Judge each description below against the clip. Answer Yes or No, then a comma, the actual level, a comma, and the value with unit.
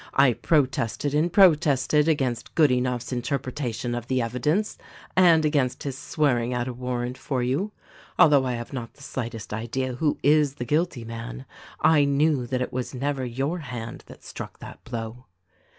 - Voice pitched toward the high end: No, low, 130 Hz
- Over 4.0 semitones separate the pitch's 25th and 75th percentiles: No, average, 3.4 semitones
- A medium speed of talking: Yes, average, 165 wpm